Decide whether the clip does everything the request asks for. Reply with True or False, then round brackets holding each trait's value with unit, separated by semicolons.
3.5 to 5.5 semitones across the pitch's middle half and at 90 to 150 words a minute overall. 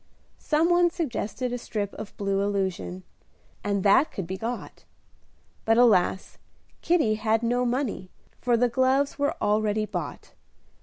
True (4.2 semitones; 140 wpm)